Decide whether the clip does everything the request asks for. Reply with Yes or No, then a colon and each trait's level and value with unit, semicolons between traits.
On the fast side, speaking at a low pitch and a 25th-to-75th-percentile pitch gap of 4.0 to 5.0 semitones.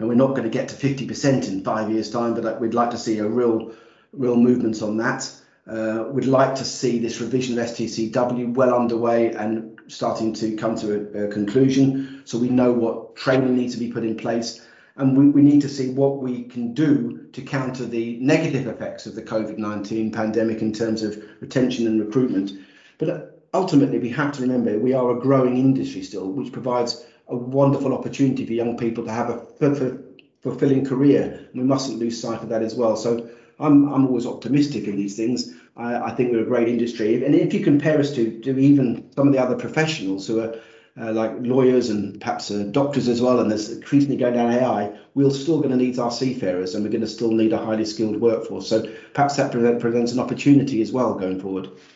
No: fast, 215 wpm; low, 120 Hz; average, 2.8 semitones